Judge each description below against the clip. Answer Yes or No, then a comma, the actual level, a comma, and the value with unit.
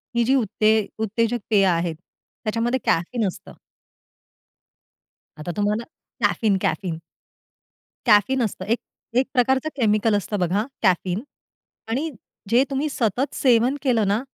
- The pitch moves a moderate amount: Yes, average, 3.6 semitones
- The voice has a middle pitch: No, high, 220 Hz